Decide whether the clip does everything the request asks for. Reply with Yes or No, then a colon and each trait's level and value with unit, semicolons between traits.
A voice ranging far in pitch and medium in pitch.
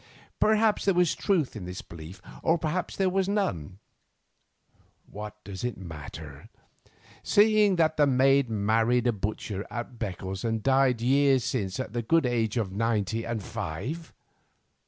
No: wide, 7.4 semitones; low, 120 Hz